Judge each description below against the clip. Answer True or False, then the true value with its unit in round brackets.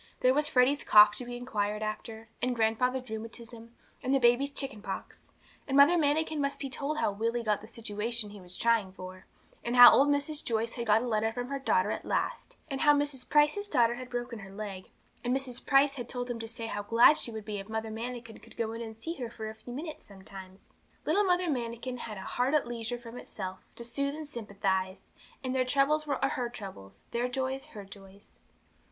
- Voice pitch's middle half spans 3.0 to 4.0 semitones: True (3.7 semitones)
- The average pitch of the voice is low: False (240 Hz)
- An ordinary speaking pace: False (220 wpm)